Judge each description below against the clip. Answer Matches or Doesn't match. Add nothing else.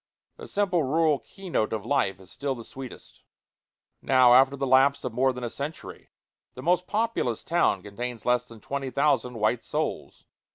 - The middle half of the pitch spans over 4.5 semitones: Doesn't match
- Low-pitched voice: Matches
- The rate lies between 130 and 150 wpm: Doesn't match